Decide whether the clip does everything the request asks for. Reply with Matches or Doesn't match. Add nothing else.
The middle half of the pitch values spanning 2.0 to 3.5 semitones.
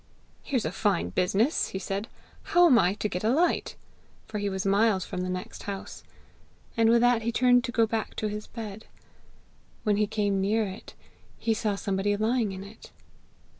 Matches